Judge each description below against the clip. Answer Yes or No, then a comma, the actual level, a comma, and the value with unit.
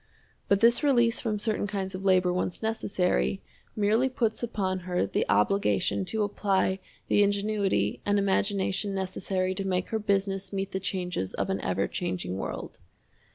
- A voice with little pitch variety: Yes, narrow, 2.1 semitones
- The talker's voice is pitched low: No, high, 195 Hz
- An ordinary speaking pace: Yes, average, 155 wpm